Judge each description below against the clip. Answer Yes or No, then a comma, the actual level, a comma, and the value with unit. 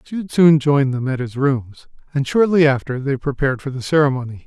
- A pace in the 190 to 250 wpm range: Yes, average, 200 wpm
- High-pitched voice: No, medium, 140 Hz